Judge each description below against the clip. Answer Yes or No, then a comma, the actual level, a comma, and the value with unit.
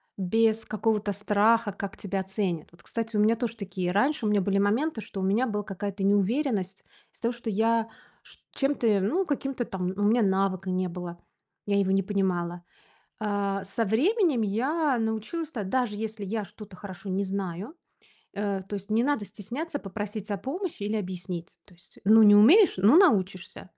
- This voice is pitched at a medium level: No, high, 205 Hz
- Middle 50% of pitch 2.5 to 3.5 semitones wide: Yes, average, 3.0 semitones